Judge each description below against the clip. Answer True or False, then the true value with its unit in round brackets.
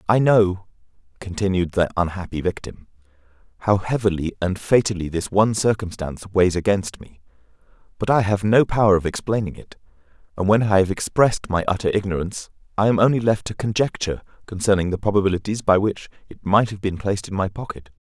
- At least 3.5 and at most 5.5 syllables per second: False (6.0 syllables/s)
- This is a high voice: False (100 Hz)